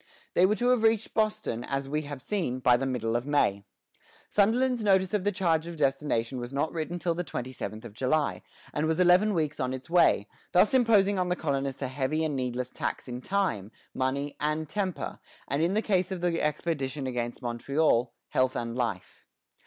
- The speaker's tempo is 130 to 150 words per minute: No, average, 195 wpm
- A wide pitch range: Yes, wide, 6.1 semitones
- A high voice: No, medium, 150 Hz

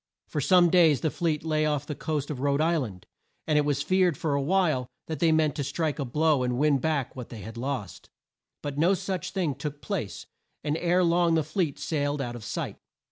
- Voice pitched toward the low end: No, medium, 150 Hz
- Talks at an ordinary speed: No, fast, 225 wpm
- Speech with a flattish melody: No, average, 3.0 semitones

